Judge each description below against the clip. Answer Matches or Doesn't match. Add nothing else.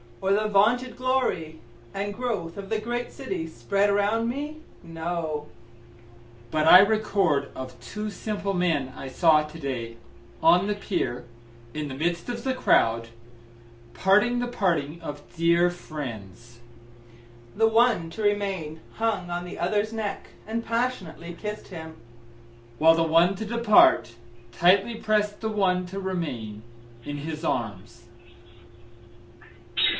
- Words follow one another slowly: Matches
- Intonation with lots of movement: Matches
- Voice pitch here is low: Doesn't match